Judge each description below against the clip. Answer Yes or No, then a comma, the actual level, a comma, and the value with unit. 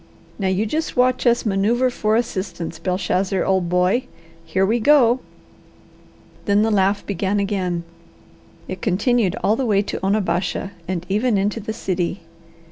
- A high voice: Yes, high, 200 Hz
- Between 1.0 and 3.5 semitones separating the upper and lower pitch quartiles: Yes, average, 3.2 semitones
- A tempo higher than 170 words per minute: No, average, 145 wpm